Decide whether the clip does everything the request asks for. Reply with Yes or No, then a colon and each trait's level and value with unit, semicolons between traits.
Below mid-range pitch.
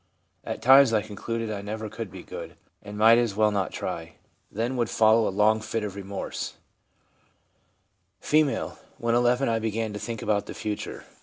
Yes: low, 110 Hz